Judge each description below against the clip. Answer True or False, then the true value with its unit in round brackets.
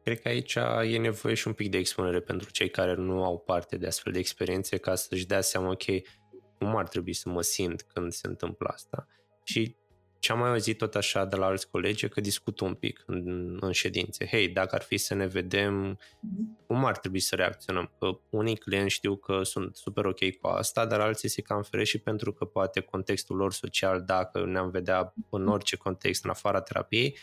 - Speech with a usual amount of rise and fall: False (2.3 semitones)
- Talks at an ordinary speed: False (210 wpm)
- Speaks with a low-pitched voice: True (95 Hz)